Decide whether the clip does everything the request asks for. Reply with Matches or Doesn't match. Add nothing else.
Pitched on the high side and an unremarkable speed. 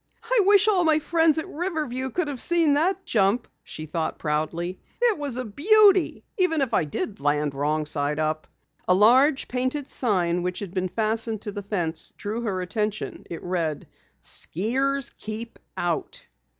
Matches